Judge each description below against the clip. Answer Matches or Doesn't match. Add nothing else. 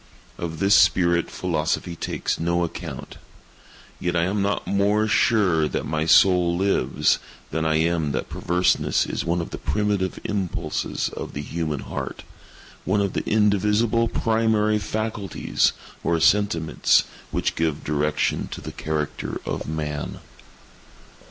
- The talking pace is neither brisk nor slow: Doesn't match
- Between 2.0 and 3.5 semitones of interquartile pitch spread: Doesn't match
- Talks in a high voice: Doesn't match